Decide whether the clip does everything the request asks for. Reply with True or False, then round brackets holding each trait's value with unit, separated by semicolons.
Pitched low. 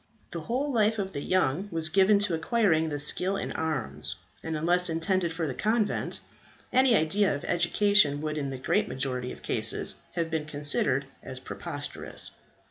False (165 Hz)